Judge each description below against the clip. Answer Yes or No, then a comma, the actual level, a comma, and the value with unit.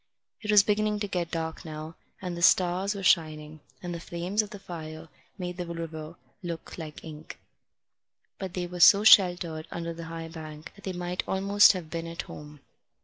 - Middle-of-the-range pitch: Yes, medium, 170 Hz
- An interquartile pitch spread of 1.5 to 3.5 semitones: Yes, average, 2.8 semitones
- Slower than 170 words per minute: No, average, 190 wpm